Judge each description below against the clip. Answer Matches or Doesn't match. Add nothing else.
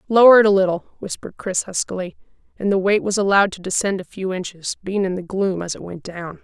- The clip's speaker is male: Doesn't match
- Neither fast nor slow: Doesn't match